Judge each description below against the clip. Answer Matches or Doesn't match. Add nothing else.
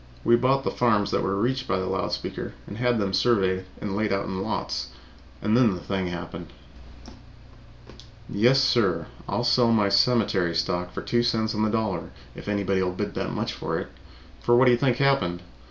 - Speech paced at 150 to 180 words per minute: Doesn't match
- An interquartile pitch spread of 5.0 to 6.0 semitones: Doesn't match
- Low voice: Matches